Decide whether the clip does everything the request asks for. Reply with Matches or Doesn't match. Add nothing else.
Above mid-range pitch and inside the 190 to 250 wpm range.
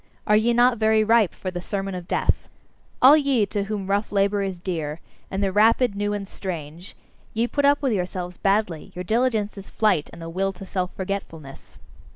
Matches